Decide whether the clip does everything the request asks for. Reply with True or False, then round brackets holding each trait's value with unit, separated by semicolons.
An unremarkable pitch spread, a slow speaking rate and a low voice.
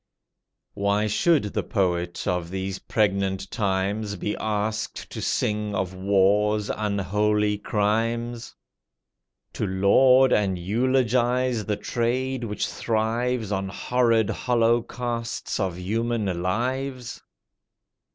True (3.3 semitones; 100 wpm; 105 Hz)